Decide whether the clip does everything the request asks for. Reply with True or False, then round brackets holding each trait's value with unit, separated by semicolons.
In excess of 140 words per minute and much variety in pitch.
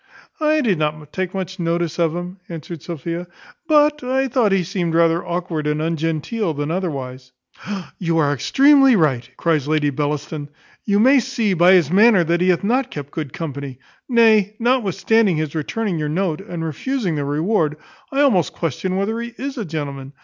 True (175 wpm; 6.1 semitones)